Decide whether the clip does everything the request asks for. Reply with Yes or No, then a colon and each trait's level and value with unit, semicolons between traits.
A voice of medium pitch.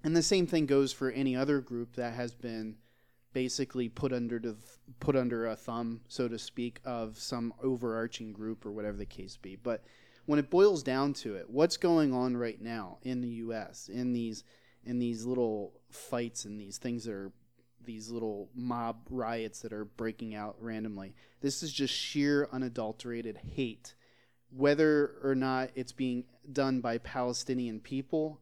No: low, 120 Hz